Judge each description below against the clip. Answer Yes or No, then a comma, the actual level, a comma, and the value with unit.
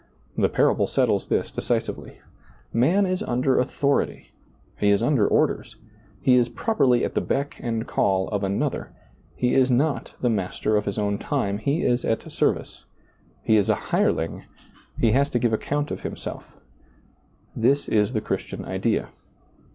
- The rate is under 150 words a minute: No, average, 160 wpm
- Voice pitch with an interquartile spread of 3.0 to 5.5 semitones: Yes, average, 4.6 semitones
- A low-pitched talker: Yes, low, 120 Hz